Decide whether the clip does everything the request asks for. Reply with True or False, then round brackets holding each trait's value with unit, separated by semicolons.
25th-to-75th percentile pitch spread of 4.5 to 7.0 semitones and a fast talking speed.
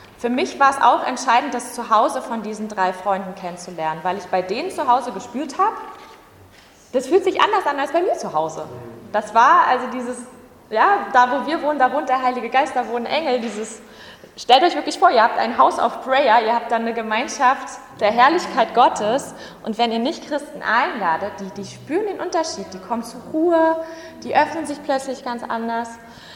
True (5.0 semitones; 200 wpm)